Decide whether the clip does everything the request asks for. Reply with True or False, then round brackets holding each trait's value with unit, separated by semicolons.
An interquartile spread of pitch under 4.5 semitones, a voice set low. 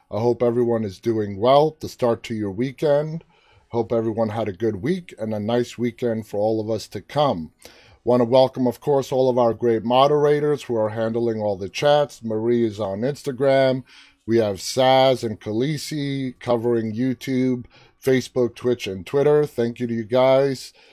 True (2.9 semitones; 120 Hz)